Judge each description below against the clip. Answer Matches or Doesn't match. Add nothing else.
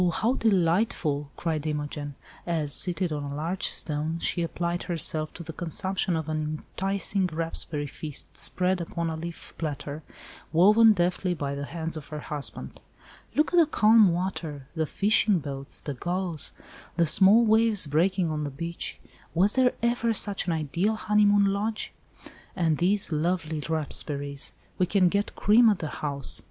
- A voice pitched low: Doesn't match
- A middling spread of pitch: Matches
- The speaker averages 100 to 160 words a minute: Matches